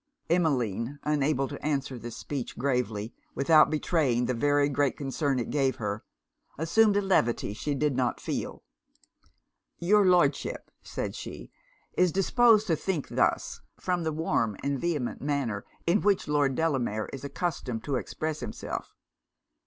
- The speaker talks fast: No, average, 145 wpm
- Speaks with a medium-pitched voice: Yes, medium, 145 Hz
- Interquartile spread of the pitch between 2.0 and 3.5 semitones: No, average, 4.5 semitones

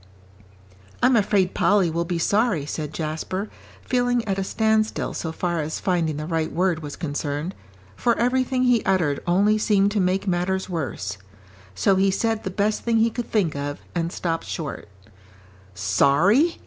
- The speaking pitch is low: No, medium, 185 Hz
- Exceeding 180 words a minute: No, average, 160 wpm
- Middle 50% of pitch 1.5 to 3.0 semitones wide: No, average, 5.1 semitones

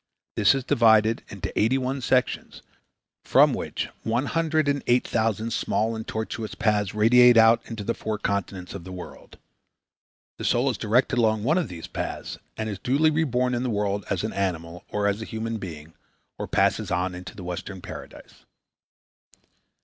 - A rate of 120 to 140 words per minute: No, average, 175 wpm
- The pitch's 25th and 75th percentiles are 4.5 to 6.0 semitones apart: No, average, 3.6 semitones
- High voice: No, low, 110 Hz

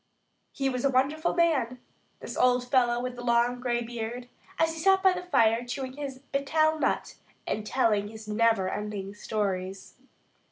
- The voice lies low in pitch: No, high, 245 Hz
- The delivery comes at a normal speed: Yes, average, 160 wpm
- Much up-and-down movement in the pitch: No, average, 3.9 semitones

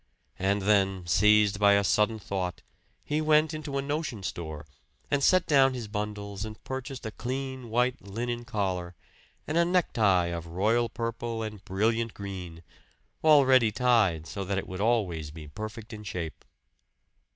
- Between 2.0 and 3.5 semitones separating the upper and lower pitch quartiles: No, average, 4.5 semitones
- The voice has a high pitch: No, low, 105 Hz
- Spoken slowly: No, average, 155 wpm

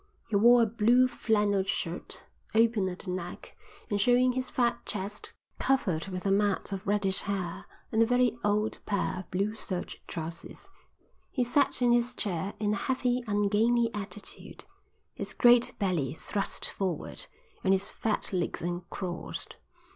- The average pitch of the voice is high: Yes, high, 205 Hz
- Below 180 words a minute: Yes, average, 155 wpm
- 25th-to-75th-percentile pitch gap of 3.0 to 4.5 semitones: Yes, average, 3.9 semitones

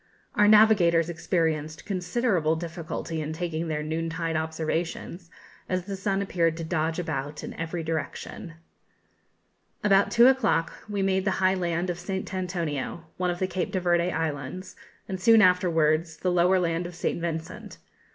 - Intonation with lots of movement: No, narrow, 2.4 semitones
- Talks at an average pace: Yes, average, 160 wpm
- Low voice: No, medium, 170 Hz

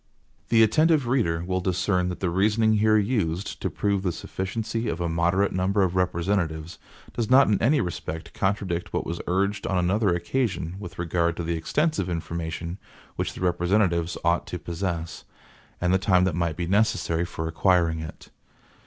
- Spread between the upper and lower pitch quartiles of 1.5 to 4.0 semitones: Yes, average, 3.3 semitones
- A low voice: Yes, very low, 90 Hz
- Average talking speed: Yes, average, 175 wpm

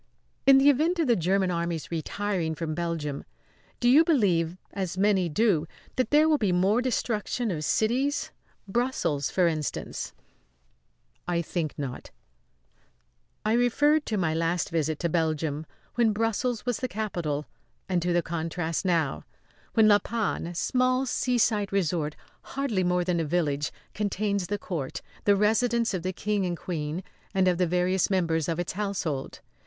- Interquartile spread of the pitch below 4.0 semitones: No, average, 5.1 semitones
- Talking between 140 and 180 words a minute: Yes, average, 160 wpm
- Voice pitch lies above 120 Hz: Yes, medium, 185 Hz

